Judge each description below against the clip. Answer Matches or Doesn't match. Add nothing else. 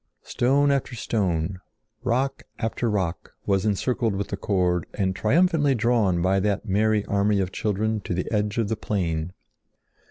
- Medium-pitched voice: Doesn't match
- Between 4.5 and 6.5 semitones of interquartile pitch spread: Doesn't match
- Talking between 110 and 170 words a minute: Matches